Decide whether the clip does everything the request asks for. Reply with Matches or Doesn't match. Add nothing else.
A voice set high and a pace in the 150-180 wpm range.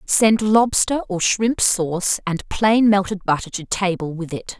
Matches